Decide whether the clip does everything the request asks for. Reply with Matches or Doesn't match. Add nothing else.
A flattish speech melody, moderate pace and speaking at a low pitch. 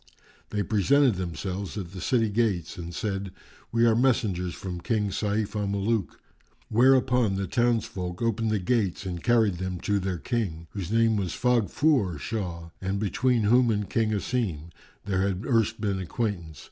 Doesn't match